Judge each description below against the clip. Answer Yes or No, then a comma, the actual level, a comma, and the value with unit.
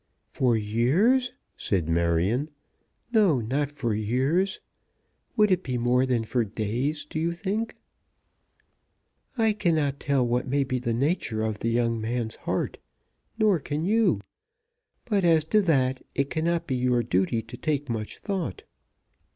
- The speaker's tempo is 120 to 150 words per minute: Yes, average, 145 wpm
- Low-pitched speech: Yes, low, 130 Hz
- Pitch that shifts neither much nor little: No, wide, 6.5 semitones